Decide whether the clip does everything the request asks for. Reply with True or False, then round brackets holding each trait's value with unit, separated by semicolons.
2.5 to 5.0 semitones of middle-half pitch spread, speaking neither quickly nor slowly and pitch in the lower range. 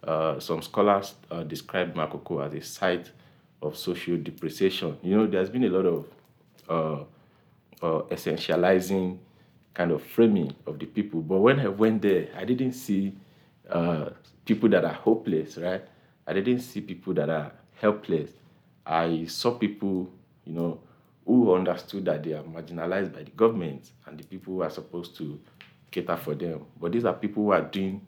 True (3.7 semitones; 170 wpm; 95 Hz)